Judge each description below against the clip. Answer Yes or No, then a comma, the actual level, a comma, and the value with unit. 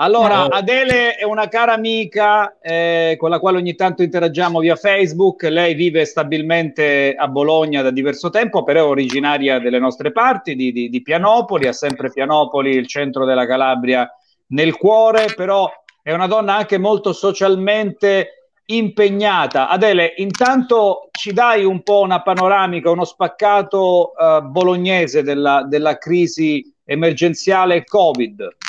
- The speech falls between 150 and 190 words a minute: No, average, 140 wpm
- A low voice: No, medium, 180 Hz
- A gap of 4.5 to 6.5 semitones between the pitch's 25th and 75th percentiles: Yes, average, 5.2 semitones